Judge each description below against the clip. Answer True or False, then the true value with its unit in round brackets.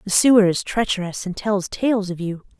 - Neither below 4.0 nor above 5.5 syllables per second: True (5.0 syllables/s)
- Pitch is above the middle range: True (200 Hz)